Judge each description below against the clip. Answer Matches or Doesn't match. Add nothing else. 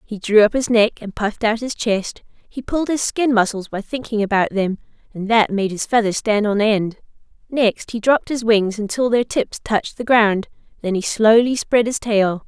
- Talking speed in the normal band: Doesn't match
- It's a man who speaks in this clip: Doesn't match